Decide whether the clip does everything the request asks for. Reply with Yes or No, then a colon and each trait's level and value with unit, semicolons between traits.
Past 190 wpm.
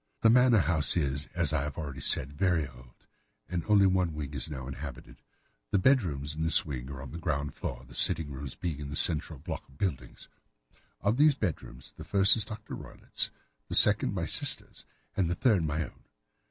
Yes: fast, 205 wpm